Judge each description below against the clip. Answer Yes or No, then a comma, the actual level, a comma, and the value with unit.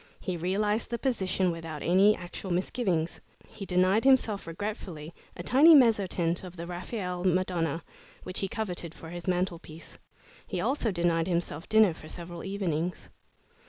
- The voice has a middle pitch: Yes, medium, 180 Hz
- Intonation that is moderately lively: Yes, average, 3.4 semitones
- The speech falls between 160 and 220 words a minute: No, average, 145 wpm